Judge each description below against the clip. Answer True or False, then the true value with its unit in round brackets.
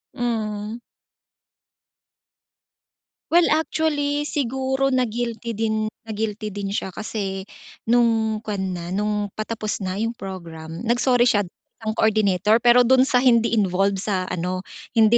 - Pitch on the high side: True (220 Hz)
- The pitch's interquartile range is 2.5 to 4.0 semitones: True (3.4 semitones)